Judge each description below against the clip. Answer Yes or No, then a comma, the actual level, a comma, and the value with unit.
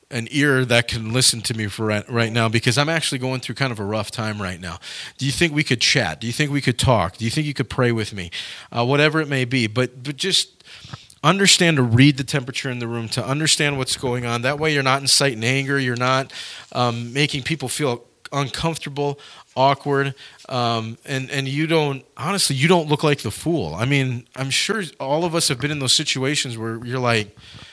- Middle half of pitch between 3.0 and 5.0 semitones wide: Yes, average, 3.5 semitones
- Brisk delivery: Yes, fast, 245 wpm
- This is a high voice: No, low, 130 Hz